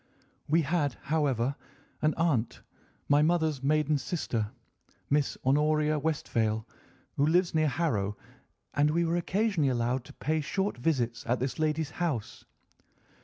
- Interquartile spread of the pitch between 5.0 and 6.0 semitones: No, average, 3.7 semitones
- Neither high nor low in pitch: Yes, medium, 150 Hz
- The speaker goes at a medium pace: No, slow, 130 wpm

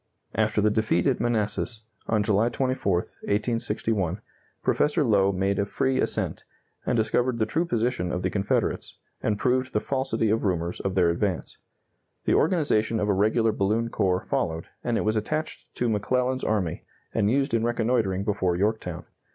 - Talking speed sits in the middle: Yes, average, 165 wpm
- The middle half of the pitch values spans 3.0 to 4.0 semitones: Yes, average, 3.4 semitones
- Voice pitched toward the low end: Yes, low, 110 Hz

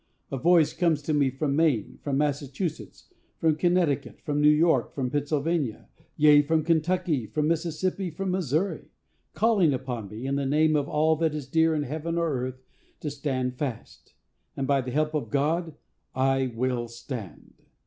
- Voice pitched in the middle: Yes, medium, 150 Hz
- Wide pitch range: No, average, 3.4 semitones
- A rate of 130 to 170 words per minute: Yes, average, 160 wpm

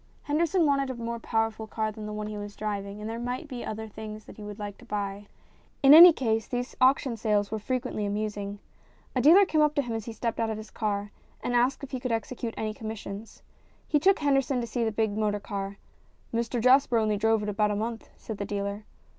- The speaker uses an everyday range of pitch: Yes, average, 3.2 semitones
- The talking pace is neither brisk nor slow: No, fast, 240 wpm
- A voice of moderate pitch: No, high, 225 Hz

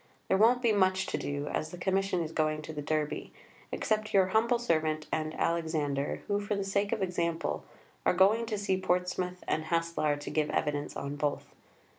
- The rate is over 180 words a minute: Yes, average, 190 wpm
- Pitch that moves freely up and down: No, average, 4.3 semitones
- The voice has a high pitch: No, medium, 175 Hz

